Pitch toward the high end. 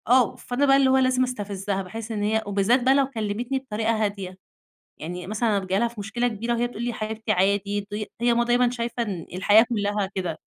Yes: high, 220 Hz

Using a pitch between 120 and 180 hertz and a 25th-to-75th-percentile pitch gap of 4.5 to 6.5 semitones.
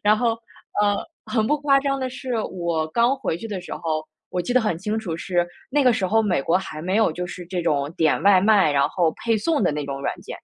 No: high, 190 Hz; average, 5.3 semitones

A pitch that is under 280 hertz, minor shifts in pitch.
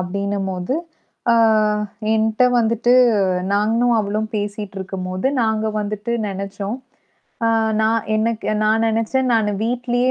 Yes: high, 215 Hz; narrow, 2.2 semitones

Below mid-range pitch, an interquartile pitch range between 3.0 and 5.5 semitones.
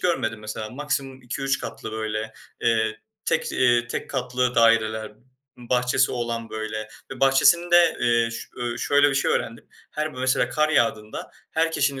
Yes: low, 120 Hz; average, 3.3 semitones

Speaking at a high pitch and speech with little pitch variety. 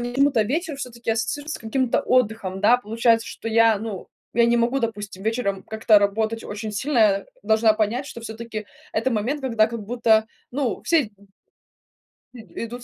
Yes: high, 225 Hz; narrow, 2.2 semitones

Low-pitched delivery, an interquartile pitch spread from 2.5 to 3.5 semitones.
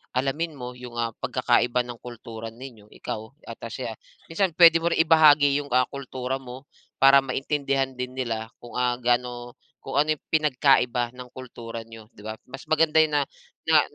Yes: low, 125 Hz; average, 3.1 semitones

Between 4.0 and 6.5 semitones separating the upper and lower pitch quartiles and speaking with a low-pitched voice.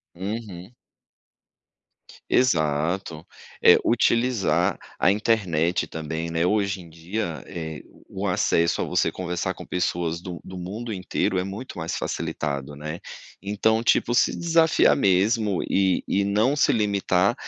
Yes: average, 4.3 semitones; very low, 95 Hz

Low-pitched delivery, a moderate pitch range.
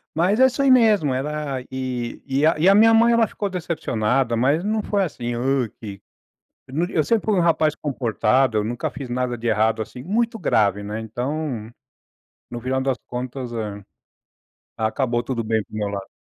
No: low, 130 Hz; wide, 6.4 semitones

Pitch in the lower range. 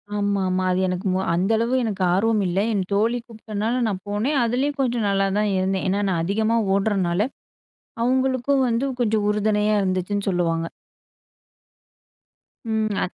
No: high, 210 Hz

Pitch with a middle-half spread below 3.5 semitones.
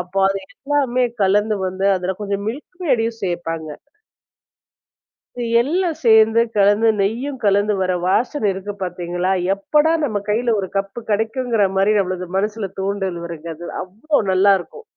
No: average, 3.8 semitones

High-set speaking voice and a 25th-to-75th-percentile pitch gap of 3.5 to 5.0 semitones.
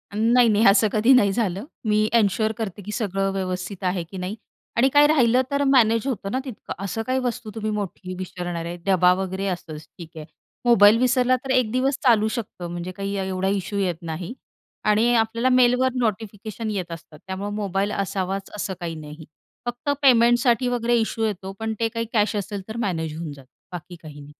Yes: high, 205 Hz; average, 4.1 semitones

